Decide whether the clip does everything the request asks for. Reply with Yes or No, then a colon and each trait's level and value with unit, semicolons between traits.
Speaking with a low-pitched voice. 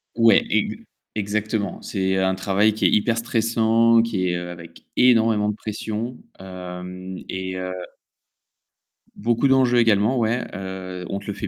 Yes: low, 105 Hz